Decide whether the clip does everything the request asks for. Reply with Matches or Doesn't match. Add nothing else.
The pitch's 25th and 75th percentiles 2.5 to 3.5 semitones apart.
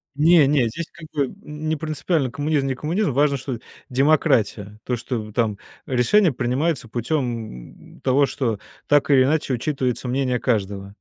Doesn't match